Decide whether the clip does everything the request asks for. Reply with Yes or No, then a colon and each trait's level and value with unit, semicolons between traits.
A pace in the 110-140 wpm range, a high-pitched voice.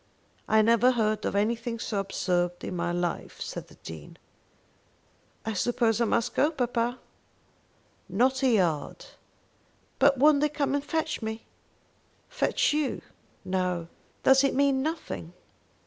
Yes: slow, 135 wpm; high, 230 Hz